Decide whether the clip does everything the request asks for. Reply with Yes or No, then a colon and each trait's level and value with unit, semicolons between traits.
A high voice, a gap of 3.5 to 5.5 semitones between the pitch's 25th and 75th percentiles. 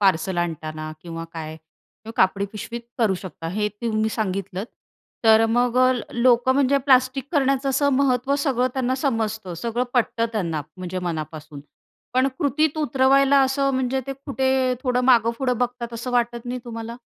Yes: high, 235 Hz; average, 5.0 semitones